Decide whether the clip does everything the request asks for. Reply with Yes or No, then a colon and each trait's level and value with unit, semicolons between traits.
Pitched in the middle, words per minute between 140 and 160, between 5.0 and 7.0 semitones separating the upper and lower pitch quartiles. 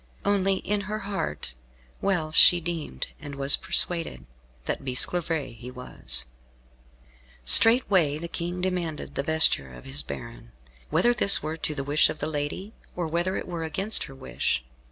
Yes: medium, 160 Hz; average, 155 wpm; average, 5.3 semitones